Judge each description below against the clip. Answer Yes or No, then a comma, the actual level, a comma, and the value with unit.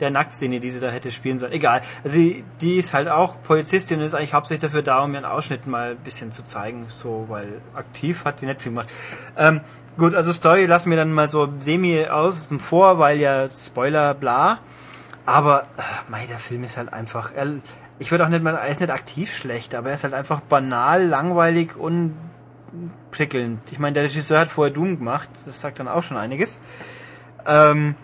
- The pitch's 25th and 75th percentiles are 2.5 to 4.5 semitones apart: Yes, average, 4.2 semitones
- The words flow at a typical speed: No, fast, 210 wpm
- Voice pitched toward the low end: No, medium, 145 Hz